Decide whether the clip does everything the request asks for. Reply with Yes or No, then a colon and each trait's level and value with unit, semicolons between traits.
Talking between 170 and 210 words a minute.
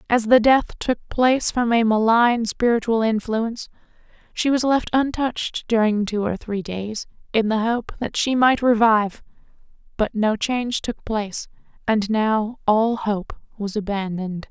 No: average, 155 wpm